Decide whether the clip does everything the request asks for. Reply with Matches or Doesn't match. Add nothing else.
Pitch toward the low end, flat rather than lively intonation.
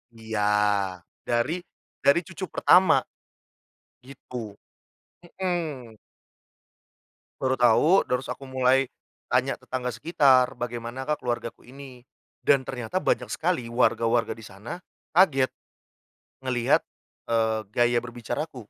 Doesn't match